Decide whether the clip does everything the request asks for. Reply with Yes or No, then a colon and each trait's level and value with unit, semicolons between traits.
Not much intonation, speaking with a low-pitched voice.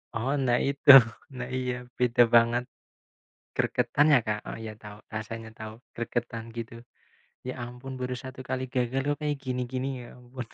Yes: narrow, 1.9 semitones; low, 125 Hz